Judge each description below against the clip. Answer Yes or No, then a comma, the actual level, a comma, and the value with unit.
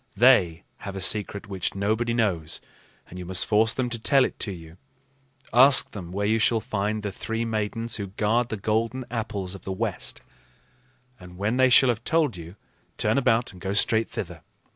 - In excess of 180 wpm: Yes, average, 190 wpm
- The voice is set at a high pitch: No, low, 110 Hz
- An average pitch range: Yes, average, 3.3 semitones